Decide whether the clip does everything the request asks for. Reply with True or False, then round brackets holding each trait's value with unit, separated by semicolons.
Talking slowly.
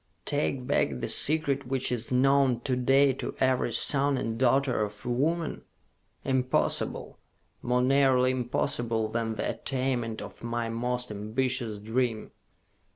True (130 wpm)